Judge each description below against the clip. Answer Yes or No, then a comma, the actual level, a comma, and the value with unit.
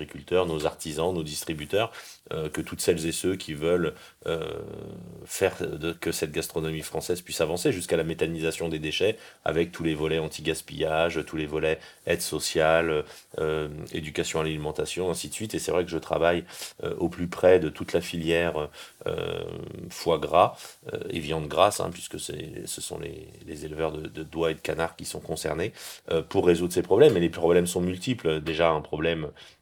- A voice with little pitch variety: Yes, narrow, 1.4 semitones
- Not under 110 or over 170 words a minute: No, average, 195 wpm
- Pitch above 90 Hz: No, very low, 80 Hz